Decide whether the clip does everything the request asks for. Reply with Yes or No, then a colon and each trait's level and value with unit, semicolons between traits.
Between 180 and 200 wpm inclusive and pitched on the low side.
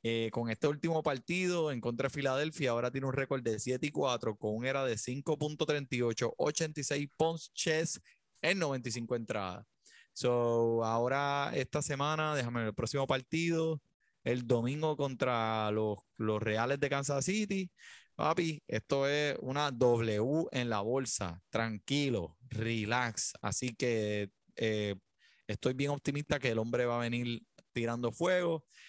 No: average, 145 wpm; low, 130 Hz